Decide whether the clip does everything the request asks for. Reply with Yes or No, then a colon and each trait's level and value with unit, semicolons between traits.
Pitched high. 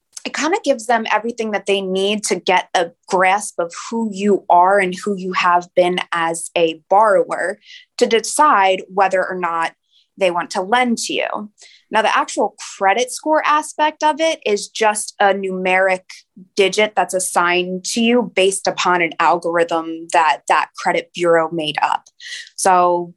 Yes: high, 195 Hz